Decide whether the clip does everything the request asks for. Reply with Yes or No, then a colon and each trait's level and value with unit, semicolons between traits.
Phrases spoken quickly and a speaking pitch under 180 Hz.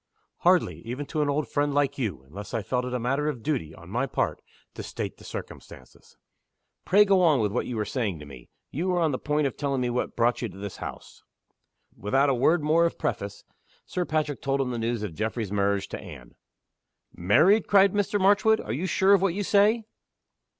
Yes: fast, 220 wpm; low, 135 Hz